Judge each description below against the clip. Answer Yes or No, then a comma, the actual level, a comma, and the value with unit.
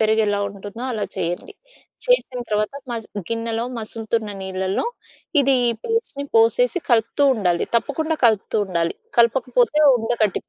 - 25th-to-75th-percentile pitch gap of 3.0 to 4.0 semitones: Yes, average, 3.3 semitones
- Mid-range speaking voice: No, high, 225 Hz